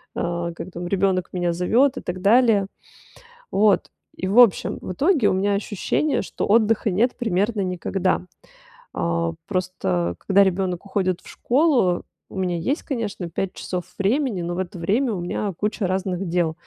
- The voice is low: No, high, 190 Hz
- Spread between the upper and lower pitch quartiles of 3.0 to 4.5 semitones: Yes, average, 3.3 semitones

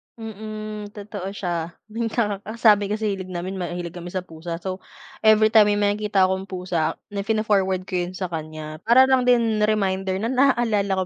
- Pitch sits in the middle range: No, high, 200 Hz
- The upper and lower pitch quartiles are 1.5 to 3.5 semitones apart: Yes, average, 2.9 semitones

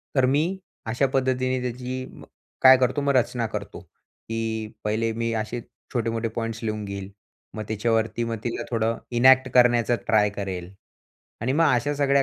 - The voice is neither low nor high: No, low, 115 Hz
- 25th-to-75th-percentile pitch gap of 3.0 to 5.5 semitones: No, narrow, 2.5 semitones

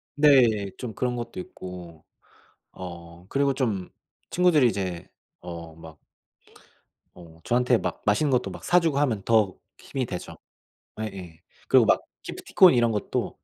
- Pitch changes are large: Yes, wide, 6.7 semitones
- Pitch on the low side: Yes, low, 110 Hz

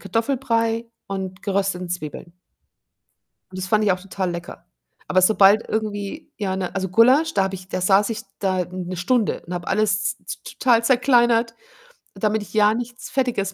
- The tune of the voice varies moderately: Yes, average, 3.5 semitones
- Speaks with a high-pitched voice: Yes, high, 205 Hz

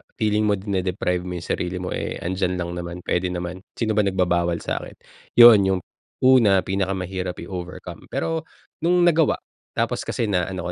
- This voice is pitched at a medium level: No, very low, 95 Hz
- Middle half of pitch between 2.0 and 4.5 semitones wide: Yes, average, 2.9 semitones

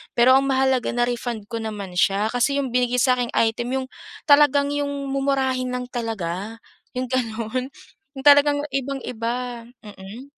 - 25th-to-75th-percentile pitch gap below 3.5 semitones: Yes, average, 3.0 semitones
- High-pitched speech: Yes, very high, 250 Hz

